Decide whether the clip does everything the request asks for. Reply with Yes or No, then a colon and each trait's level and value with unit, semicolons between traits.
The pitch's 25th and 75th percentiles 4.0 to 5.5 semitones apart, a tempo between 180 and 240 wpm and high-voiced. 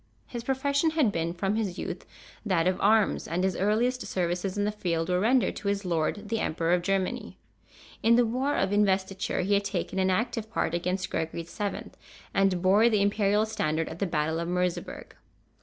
No: average, 3.5 semitones; average, 190 wpm; high, 195 Hz